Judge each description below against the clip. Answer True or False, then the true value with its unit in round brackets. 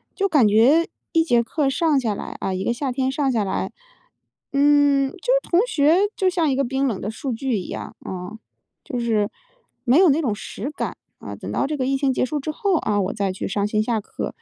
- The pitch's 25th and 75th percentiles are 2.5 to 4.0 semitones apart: False (5.2 semitones)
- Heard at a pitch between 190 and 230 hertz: False (265 Hz)